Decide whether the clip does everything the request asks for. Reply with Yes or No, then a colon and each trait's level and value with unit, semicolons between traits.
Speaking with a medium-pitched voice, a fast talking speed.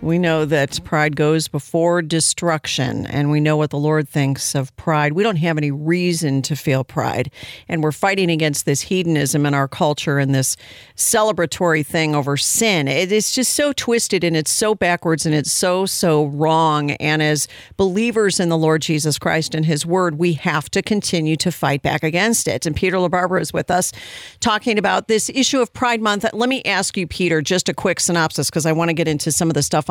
Yes: medium, 160 Hz; fast, 210 wpm